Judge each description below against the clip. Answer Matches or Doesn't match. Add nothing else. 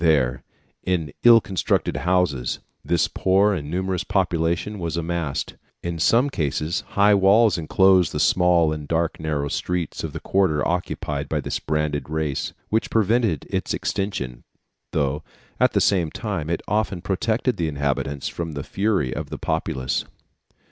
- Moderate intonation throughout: Matches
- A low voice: Matches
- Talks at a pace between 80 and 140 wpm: Doesn't match